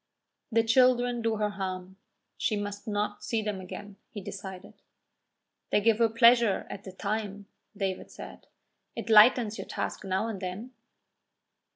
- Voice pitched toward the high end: Yes, high, 210 Hz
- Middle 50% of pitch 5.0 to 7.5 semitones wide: No, average, 2.7 semitones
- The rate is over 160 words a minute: No, average, 150 wpm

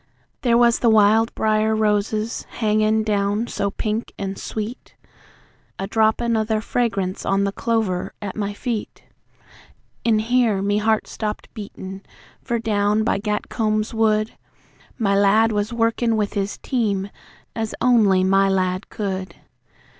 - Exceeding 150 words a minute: No, average, 140 wpm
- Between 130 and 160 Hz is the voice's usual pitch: No, high, 215 Hz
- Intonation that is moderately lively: No, narrow, 1.9 semitones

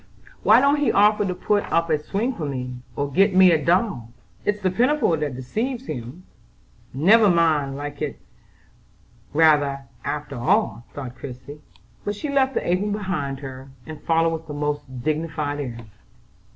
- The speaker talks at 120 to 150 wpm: No, average, 165 wpm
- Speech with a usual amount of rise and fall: No, wide, 6.4 semitones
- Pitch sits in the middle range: Yes, medium, 160 Hz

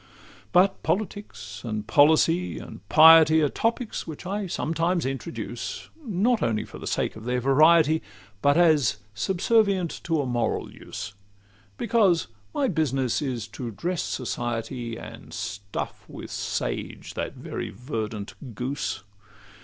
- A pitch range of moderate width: No, wide, 6.7 semitones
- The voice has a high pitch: No, medium, 150 Hz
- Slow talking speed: Yes, slow, 130 wpm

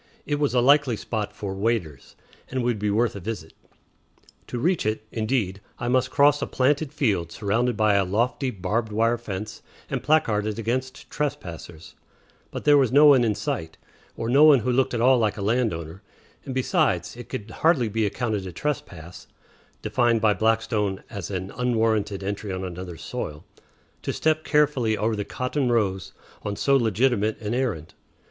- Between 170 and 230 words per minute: Yes, average, 175 wpm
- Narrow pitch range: No, average, 4.2 semitones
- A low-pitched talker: Yes, low, 115 Hz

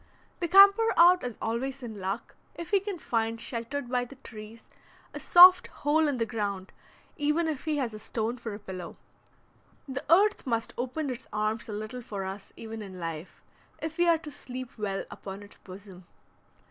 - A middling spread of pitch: No, wide, 6.1 semitones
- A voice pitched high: Yes, high, 240 Hz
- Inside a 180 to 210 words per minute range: Yes, average, 185 wpm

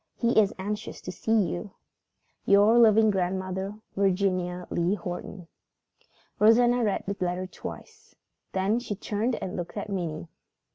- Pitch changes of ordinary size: Yes, average, 3.1 semitones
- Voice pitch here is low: No, high, 200 Hz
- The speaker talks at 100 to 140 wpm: Yes, slow, 135 wpm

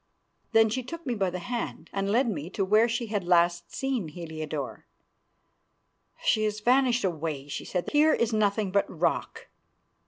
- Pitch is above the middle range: Yes, high, 205 Hz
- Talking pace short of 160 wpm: No, average, 165 wpm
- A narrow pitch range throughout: No, average, 5.3 semitones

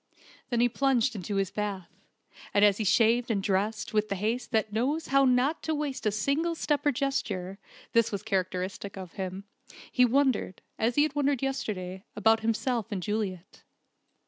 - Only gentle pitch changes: No, average, 5.0 semitones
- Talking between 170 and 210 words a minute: Yes, average, 175 wpm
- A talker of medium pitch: No, high, 220 Hz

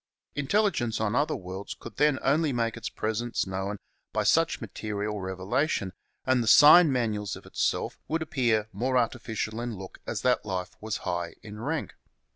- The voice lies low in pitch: Yes, low, 115 Hz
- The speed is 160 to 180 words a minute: Yes, average, 170 wpm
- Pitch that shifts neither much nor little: Yes, average, 4.3 semitones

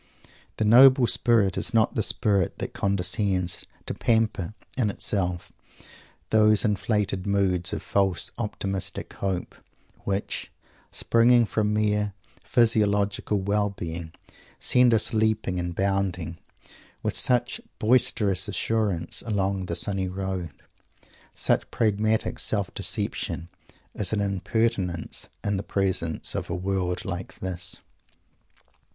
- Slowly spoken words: Yes, slow, 115 wpm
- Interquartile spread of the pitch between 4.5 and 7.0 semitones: No, average, 2.8 semitones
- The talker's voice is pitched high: No, low, 100 Hz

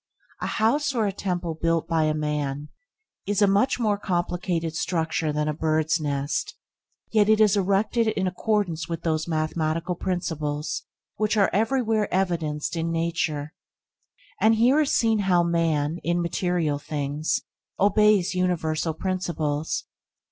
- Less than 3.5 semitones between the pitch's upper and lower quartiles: No, average, 4.4 semitones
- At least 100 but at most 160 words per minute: Yes, slow, 135 wpm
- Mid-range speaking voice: Yes, medium, 170 Hz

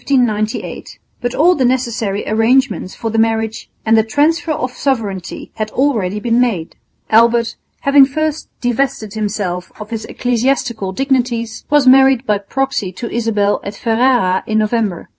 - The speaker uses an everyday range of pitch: Yes, average, 3.7 semitones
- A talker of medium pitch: No, high, 230 Hz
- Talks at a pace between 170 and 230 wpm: No, average, 140 wpm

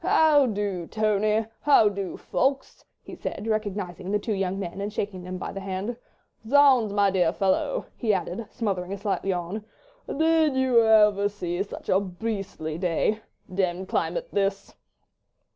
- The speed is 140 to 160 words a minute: Yes, average, 155 wpm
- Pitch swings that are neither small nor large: Yes, average, 3.0 semitones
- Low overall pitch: No, high, 200 Hz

